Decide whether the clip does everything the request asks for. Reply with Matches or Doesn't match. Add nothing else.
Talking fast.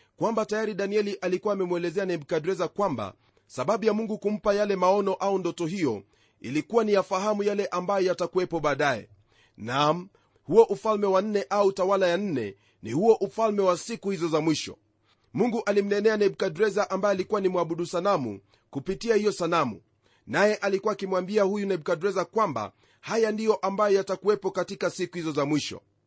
Matches